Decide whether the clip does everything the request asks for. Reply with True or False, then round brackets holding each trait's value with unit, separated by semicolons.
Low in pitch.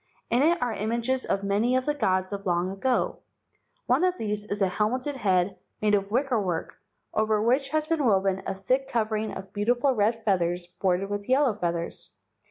False (215 Hz)